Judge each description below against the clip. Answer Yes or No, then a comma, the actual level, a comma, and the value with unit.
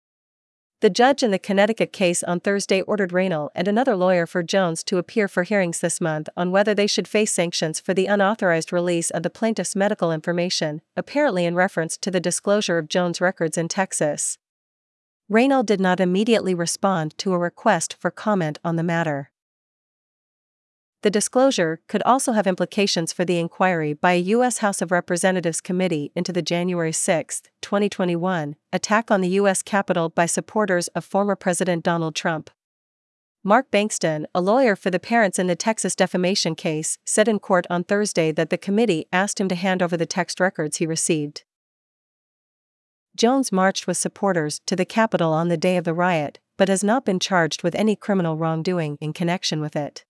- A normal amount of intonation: Yes, average, 3.0 semitones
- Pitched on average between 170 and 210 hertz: Yes, medium, 185 Hz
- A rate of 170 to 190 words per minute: Yes, average, 180 wpm